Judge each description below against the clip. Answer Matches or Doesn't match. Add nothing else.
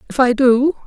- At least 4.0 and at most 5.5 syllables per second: Matches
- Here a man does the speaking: Matches